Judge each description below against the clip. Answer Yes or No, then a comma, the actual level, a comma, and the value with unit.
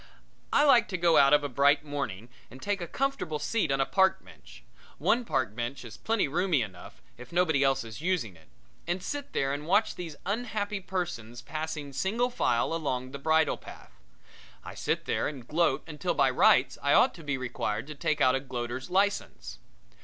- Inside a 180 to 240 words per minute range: Yes, average, 195 wpm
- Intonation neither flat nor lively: No, wide, 6.0 semitones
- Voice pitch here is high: No, medium, 150 Hz